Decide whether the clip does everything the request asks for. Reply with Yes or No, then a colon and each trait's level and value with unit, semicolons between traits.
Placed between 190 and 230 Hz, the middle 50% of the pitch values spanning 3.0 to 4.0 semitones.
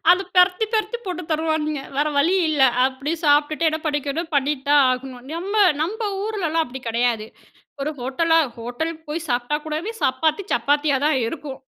No: very high, 305 Hz; average, 3.7 semitones